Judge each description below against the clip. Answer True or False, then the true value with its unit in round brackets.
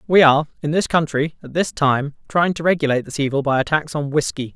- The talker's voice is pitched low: False (150 Hz)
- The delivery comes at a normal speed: False (235 wpm)